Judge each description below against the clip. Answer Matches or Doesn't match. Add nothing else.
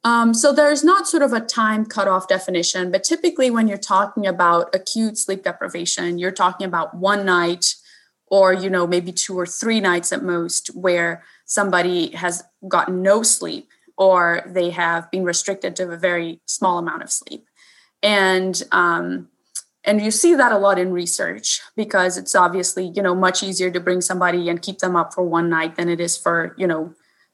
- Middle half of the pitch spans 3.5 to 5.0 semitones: Doesn't match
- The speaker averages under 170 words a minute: Doesn't match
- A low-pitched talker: Doesn't match